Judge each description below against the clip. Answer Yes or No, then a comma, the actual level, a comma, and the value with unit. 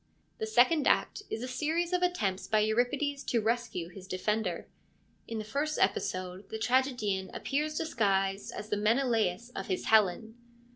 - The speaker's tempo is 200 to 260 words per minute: No, average, 155 wpm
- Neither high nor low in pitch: No, high, 220 Hz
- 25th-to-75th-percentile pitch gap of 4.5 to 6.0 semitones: Yes, average, 5.1 semitones